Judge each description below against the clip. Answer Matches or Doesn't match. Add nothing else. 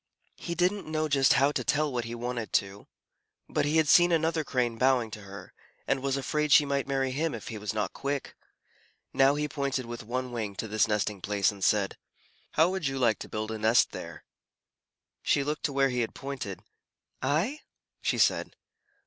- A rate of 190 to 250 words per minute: Matches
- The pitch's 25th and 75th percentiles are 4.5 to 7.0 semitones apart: Matches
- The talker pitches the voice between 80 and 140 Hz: Matches